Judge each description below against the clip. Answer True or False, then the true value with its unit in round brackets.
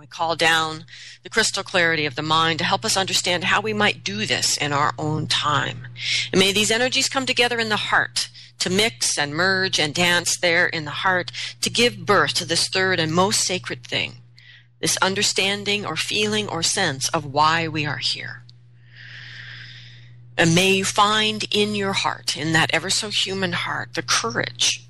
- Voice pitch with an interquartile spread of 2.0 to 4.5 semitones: False (5.1 semitones)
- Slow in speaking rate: False (185 wpm)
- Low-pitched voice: False (165 Hz)